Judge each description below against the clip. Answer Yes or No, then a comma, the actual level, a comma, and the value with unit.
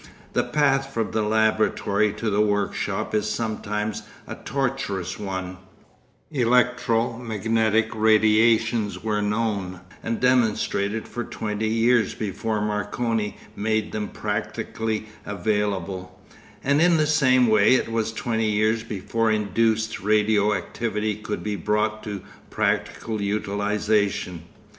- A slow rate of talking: Yes, slow, 115 wpm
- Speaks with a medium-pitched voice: No, low, 110 Hz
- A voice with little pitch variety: Yes, narrow, 1.7 semitones